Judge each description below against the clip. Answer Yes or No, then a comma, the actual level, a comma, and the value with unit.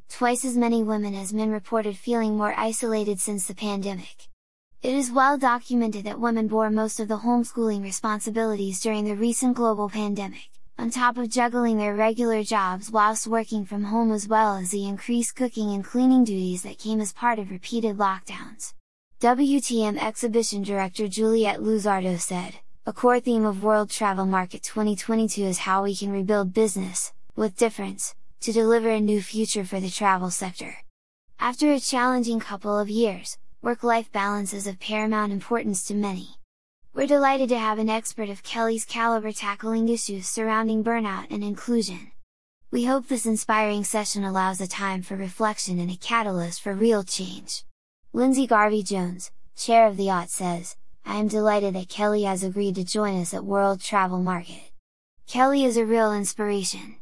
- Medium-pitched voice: No, high, 215 Hz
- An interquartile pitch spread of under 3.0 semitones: Yes, narrow, 2.6 semitones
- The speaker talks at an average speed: Yes, average, 170 wpm